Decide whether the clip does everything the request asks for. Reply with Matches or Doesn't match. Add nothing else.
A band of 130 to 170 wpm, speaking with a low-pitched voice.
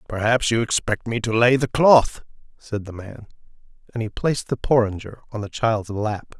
Doesn't match